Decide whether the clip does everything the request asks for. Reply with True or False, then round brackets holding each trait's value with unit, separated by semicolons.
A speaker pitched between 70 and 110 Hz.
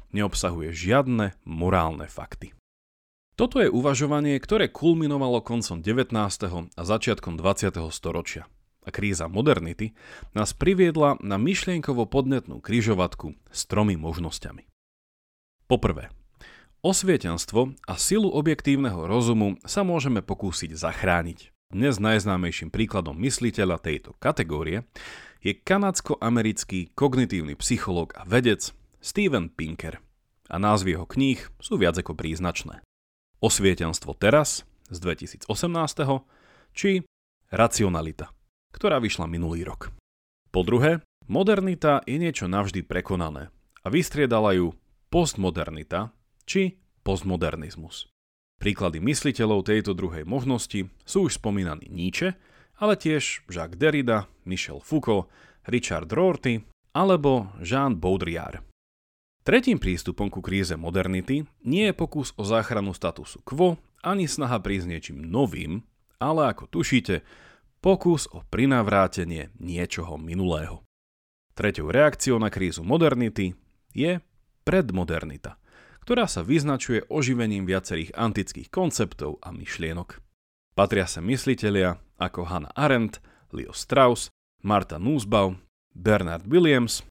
True (100 Hz)